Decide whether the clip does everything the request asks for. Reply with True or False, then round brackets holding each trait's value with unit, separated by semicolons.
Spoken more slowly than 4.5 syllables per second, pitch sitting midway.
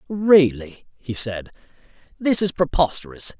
True (4.2 syllables/s; 145 Hz)